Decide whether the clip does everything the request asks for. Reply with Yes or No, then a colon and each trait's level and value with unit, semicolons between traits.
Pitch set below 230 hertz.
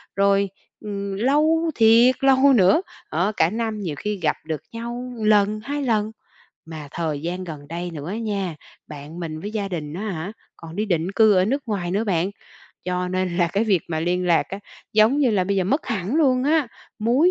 Yes: high, 200 Hz